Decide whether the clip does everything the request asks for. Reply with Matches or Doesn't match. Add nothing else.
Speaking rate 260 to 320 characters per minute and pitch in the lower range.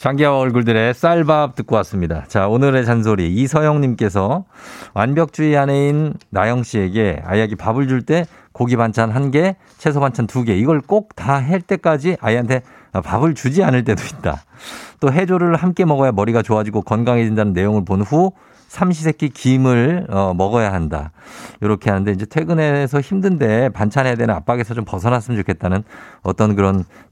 Doesn't match